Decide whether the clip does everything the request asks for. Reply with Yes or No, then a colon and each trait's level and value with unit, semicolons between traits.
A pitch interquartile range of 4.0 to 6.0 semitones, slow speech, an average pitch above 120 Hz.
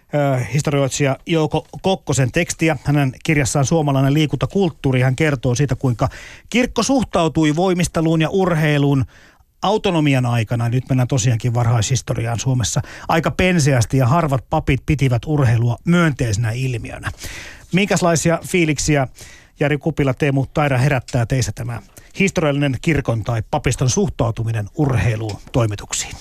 No: average, 4.4 semitones; average, 110 wpm; medium, 140 Hz